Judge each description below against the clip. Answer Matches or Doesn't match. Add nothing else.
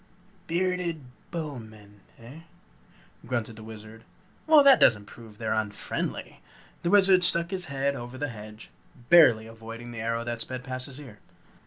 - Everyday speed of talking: Matches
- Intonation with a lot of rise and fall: Matches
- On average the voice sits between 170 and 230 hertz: Doesn't match